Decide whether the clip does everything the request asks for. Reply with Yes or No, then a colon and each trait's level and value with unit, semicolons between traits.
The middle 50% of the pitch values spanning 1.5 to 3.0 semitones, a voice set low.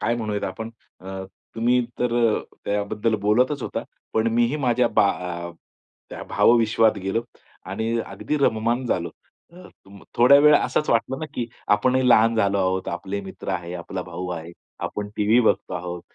No: average, 3.7 semitones; low, 110 Hz